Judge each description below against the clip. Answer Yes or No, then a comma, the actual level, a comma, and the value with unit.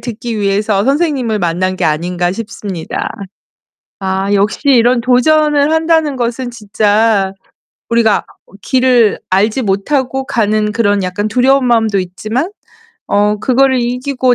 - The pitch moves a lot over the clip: No, average, 4.1 semitones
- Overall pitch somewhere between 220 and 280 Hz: Yes, high, 225 Hz